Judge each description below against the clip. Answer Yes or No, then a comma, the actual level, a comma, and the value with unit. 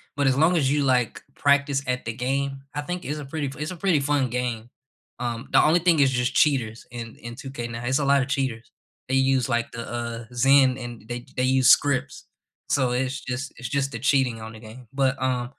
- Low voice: Yes, low, 130 Hz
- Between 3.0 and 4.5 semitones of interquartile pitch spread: No, narrow, 2.5 semitones